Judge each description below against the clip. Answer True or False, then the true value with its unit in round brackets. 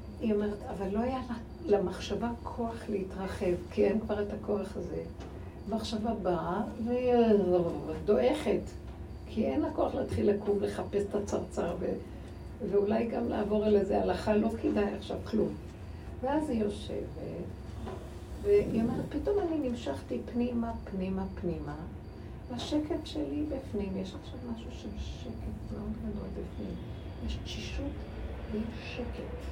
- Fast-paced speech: False (130 wpm)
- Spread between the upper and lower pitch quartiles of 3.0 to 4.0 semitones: False (4.4 semitones)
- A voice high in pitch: True (205 Hz)